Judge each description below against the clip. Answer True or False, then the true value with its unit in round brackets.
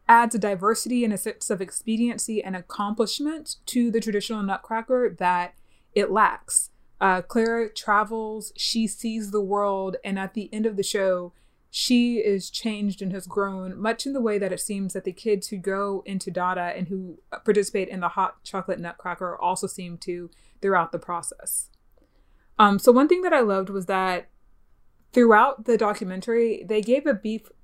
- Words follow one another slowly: False (175 wpm)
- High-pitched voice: True (205 Hz)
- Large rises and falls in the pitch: False (3.1 semitones)